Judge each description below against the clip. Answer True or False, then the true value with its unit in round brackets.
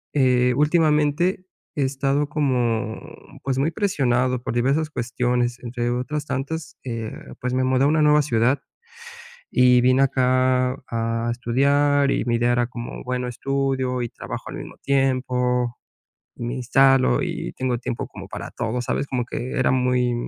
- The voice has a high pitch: False (130 Hz)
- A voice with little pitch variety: True (2.1 semitones)